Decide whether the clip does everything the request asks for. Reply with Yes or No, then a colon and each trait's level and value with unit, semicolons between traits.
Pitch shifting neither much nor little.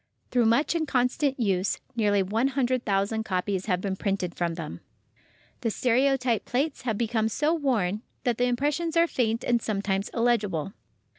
Yes: average, 4.5 semitones